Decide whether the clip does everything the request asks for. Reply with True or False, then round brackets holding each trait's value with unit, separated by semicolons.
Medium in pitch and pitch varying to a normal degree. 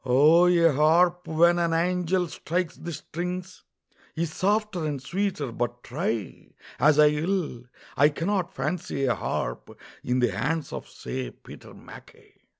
True (160 Hz; 4.7 semitones)